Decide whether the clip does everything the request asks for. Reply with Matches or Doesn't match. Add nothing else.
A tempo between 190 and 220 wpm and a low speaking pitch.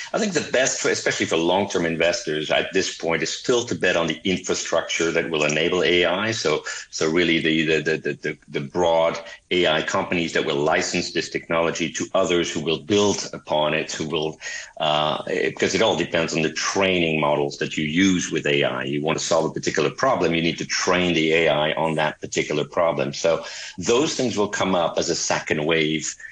Matches